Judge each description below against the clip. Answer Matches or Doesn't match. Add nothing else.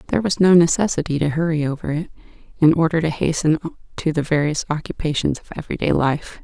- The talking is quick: Doesn't match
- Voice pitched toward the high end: Doesn't match